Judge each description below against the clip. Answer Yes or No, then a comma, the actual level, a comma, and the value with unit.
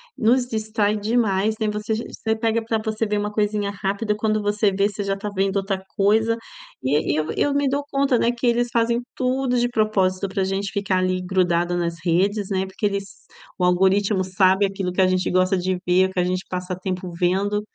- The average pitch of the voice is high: Yes, high, 200 Hz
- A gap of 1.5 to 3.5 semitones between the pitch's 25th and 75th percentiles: Yes, average, 2.8 semitones